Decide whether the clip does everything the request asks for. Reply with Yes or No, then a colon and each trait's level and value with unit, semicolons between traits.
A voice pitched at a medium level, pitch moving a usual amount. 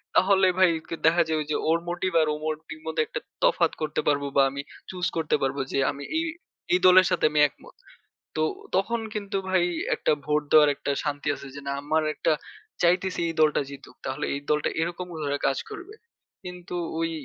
Yes: medium, 160 Hz; average, 3.5 semitones